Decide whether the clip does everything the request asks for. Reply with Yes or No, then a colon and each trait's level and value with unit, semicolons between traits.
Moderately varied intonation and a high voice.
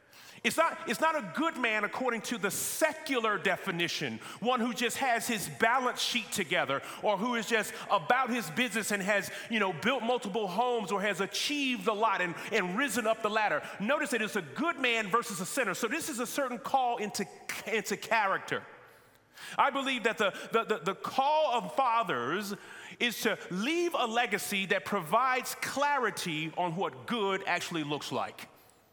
Yes: average, 3.8 semitones; high, 225 Hz